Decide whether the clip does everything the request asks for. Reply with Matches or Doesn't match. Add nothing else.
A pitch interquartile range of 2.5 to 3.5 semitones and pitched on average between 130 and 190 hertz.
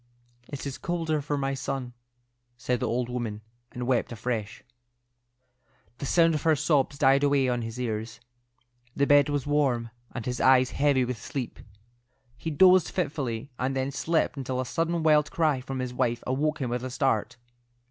Matches